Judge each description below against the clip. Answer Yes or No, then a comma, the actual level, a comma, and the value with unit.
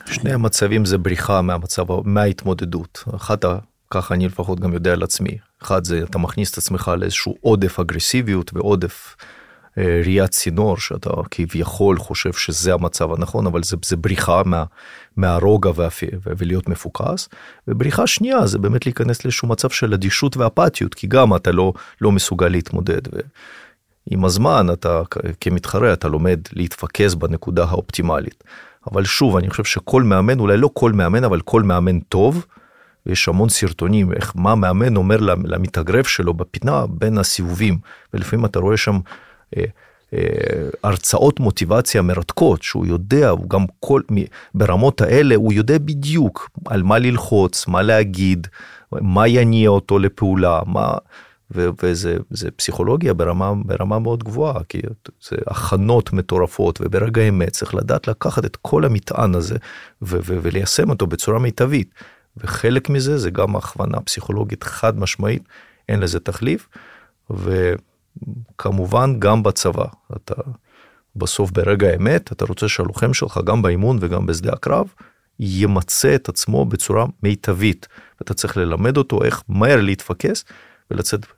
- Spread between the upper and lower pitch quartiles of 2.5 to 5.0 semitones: Yes, average, 3.7 semitones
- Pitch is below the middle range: Yes, low, 100 Hz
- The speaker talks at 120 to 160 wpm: Yes, average, 140 wpm